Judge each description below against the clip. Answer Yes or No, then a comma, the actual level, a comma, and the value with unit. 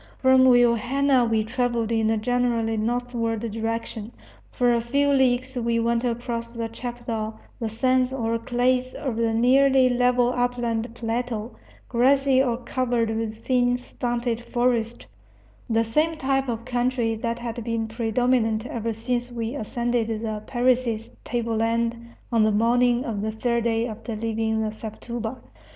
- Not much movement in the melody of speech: Yes, narrow, 1.6 semitones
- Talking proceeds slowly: No, average, 145 wpm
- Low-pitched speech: No, high, 235 Hz